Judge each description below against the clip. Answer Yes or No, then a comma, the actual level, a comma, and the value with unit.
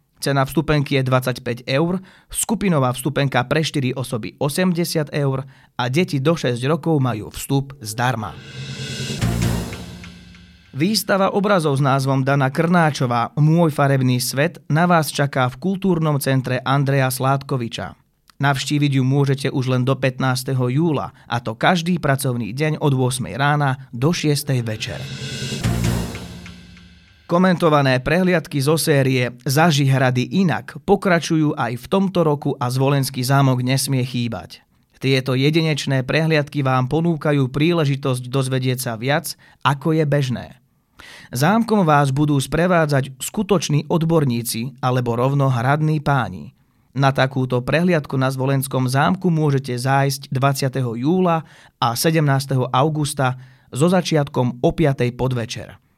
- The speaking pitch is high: No, low, 135 Hz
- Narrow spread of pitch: No, average, 3.4 semitones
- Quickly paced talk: No, average, 120 wpm